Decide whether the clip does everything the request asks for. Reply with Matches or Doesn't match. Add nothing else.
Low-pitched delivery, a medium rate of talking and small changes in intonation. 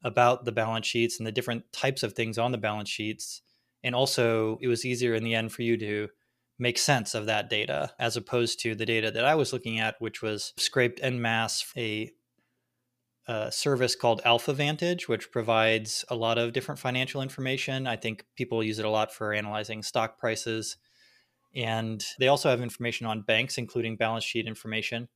Matches